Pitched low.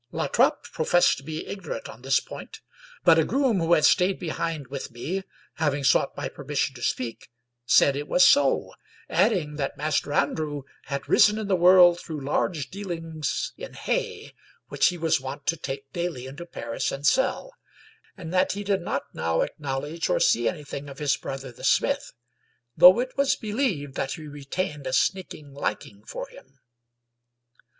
No: medium, 155 Hz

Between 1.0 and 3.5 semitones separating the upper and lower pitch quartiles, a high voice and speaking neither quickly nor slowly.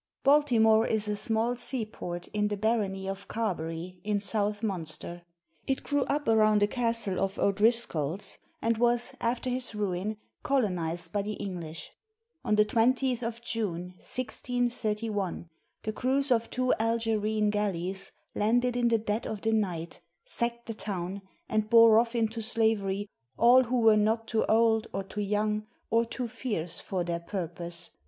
Yes: average, 3.1 semitones; high, 215 Hz; average, 155 wpm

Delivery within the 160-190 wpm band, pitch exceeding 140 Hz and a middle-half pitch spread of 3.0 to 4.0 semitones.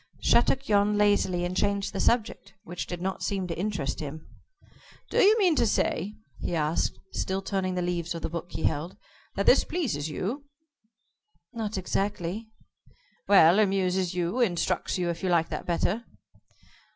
Yes: average, 165 wpm; medium, 185 Hz; average, 3.3 semitones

